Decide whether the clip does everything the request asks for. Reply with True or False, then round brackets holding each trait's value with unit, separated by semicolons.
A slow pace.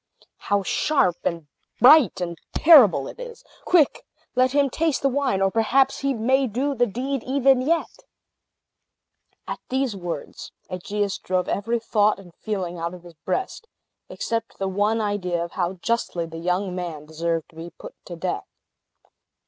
False (160 wpm)